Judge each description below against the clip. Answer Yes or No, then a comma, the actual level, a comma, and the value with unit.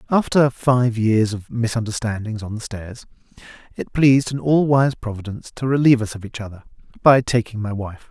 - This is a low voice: Yes, low, 115 Hz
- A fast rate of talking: No, average, 180 wpm